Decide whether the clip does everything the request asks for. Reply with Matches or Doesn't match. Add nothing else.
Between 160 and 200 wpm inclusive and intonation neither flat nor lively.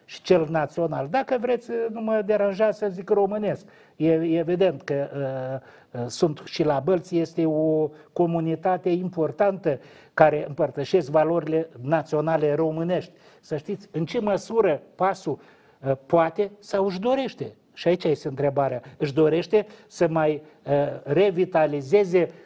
Doesn't match